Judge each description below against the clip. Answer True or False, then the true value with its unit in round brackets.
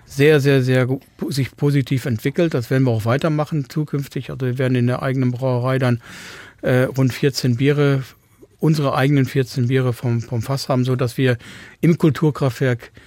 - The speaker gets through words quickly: False (165 wpm)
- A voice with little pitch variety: True (2.1 semitones)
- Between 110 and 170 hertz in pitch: True (130 Hz)